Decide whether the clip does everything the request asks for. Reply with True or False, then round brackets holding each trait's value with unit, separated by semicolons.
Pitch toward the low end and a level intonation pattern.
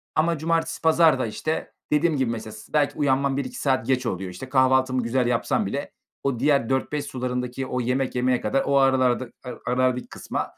True (130 Hz; 2.1 semitones)